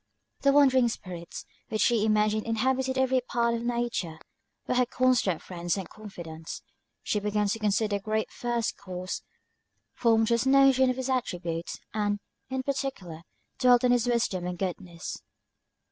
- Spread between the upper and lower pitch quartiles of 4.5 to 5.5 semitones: Yes, average, 4.8 semitones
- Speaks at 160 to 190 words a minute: No, average, 150 wpm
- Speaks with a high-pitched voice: Yes, high, 225 Hz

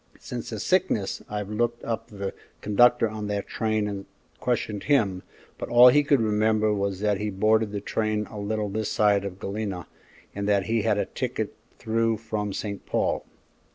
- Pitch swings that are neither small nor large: No, narrow, 1.6 semitones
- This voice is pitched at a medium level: No, low, 105 Hz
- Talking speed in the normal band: Yes, average, 180 wpm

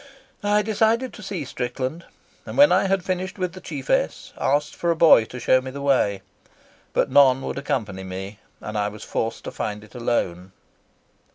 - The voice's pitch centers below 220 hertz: Yes, low, 135 Hz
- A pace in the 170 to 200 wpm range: Yes, average, 185 wpm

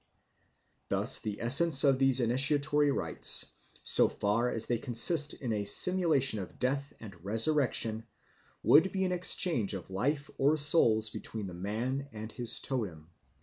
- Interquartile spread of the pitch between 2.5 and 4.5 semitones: No, average, 5.0 semitones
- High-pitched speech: No, low, 125 Hz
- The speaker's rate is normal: Yes, average, 150 wpm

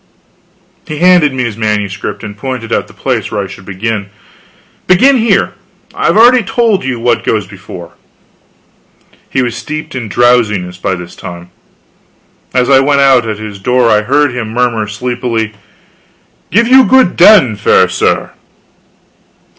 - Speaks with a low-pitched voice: Yes, low, 120 Hz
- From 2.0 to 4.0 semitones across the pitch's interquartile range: No, wide, 5.4 semitones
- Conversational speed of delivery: Yes, average, 150 wpm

